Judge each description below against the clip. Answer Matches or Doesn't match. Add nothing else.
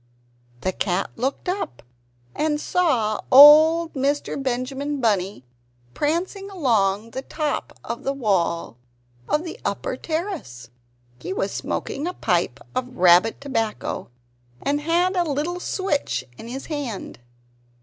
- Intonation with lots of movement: Matches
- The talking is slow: Matches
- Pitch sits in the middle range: Doesn't match